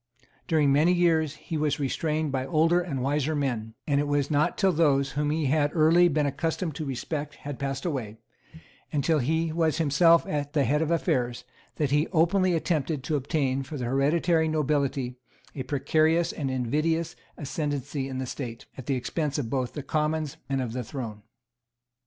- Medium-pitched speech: Yes, medium, 145 Hz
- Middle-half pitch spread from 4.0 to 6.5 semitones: No, average, 2.9 semitones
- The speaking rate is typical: Yes, average, 180 wpm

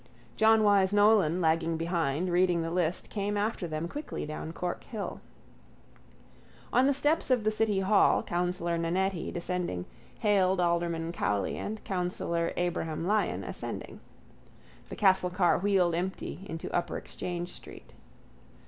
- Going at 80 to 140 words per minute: Yes, slow, 135 wpm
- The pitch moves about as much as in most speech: Yes, average, 3.2 semitones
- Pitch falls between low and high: Yes, medium, 180 Hz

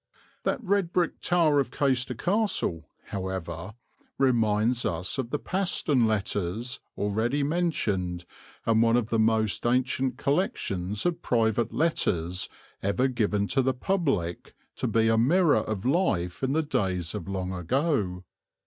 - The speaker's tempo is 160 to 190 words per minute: No, average, 140 wpm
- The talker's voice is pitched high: No, low, 115 Hz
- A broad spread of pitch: Yes, wide, 6.7 semitones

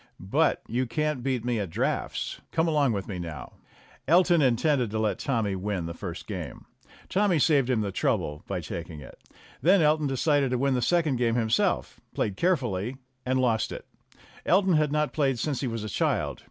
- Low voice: Yes, low, 125 Hz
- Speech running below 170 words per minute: No, average, 190 wpm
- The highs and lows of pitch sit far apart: Yes, wide, 5.9 semitones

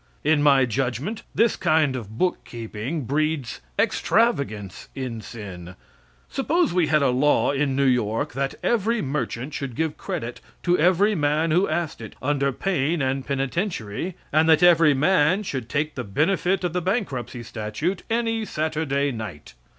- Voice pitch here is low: No, medium, 145 Hz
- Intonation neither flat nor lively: No, wide, 5.8 semitones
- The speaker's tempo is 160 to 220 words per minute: No, average, 150 wpm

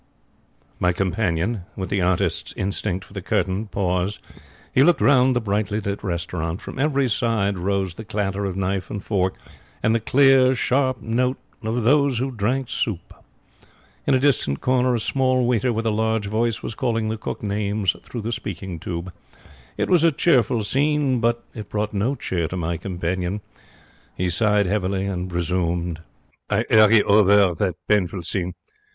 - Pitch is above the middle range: No, low, 105 Hz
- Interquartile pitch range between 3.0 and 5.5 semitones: Yes, average, 4.3 semitones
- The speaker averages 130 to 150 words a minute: No, average, 170 wpm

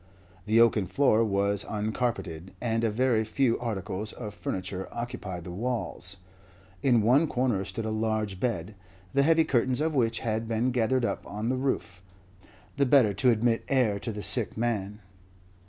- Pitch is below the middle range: Yes, low, 115 Hz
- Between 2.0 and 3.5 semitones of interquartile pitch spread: Yes, average, 3.2 semitones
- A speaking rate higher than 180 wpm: No, average, 165 wpm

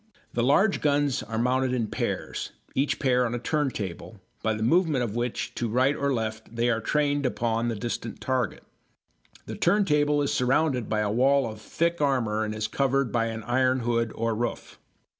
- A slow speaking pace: No, average, 185 wpm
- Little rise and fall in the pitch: No, average, 3.7 semitones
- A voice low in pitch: Yes, low, 125 Hz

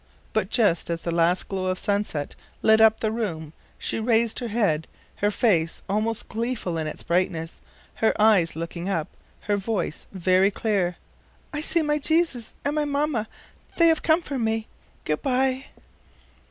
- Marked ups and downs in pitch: Yes, wide, 5.7 semitones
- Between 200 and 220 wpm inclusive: No, average, 165 wpm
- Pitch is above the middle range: Yes, high, 215 Hz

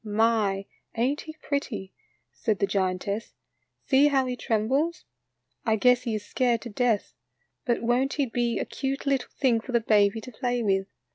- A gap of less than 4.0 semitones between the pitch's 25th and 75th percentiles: Yes, average, 3.6 semitones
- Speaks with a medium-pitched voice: No, high, 235 Hz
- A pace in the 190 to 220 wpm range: No, average, 180 wpm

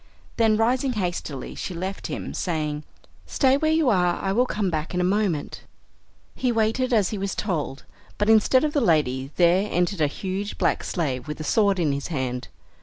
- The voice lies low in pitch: No, high, 190 Hz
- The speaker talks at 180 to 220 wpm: Yes, average, 190 wpm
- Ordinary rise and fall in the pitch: No, wide, 6.1 semitones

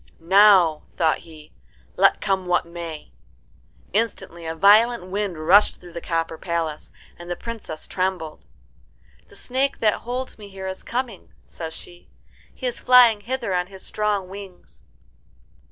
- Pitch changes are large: No, average, 4.0 semitones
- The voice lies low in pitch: No, high, 190 Hz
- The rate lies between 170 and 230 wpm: No, average, 145 wpm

